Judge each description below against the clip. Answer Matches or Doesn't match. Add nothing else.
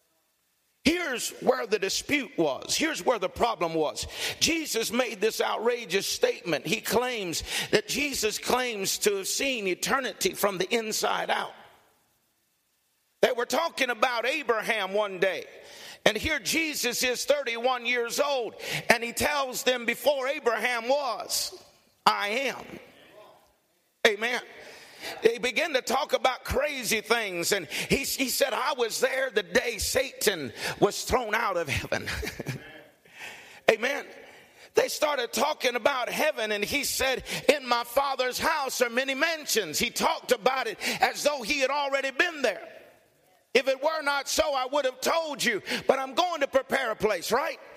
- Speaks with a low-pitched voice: Doesn't match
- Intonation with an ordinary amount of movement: Matches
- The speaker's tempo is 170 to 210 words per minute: Doesn't match